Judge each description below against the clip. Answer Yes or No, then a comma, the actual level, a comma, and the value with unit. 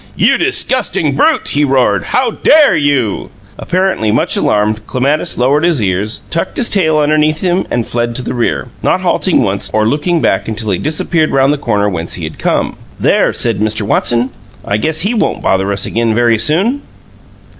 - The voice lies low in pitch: Yes, low, 130 Hz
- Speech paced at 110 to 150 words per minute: No, average, 185 wpm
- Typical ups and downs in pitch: No, wide, 6.6 semitones